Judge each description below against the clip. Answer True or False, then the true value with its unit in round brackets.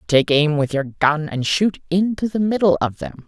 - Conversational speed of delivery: False (220 wpm)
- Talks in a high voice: False (160 Hz)